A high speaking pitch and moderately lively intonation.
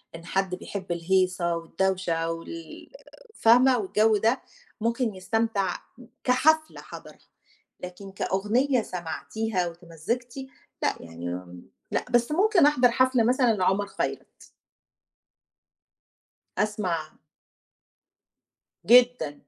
No: high, 200 Hz; wide, 5.7 semitones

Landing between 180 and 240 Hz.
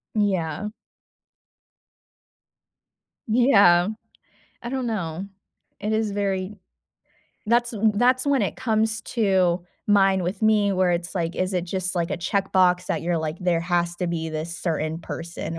Yes: medium, 185 Hz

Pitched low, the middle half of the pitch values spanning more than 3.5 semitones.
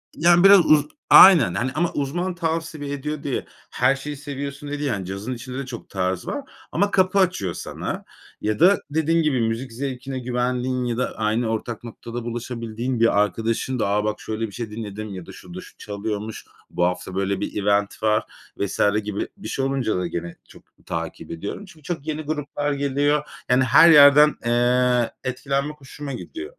Yes: low, 125 Hz; average, 5.3 semitones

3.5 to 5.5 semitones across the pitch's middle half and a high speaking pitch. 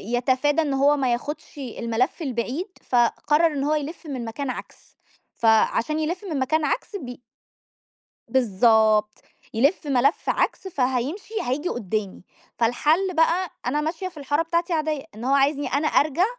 Yes: average, 4.3 semitones; very high, 280 Hz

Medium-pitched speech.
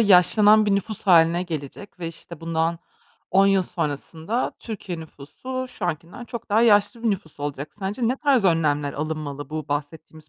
Yes: medium, 175 Hz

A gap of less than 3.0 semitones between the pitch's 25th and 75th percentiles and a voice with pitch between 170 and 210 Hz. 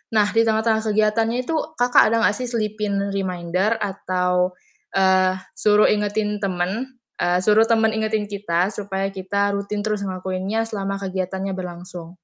Yes: narrow, 2.5 semitones; high, 200 Hz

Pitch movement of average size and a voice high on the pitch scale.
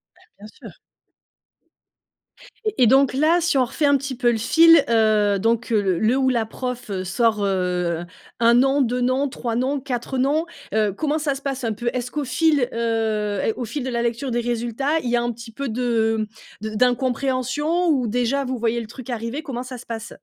Yes: average, 3.2 semitones; high, 245 Hz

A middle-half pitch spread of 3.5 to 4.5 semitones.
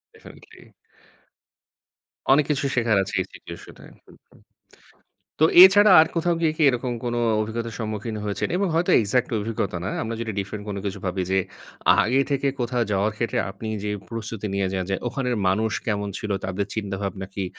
Yes: average, 3.8 semitones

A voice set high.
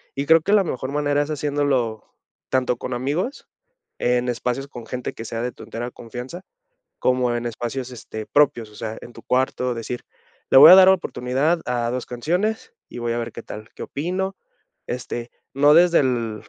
No: low, 125 Hz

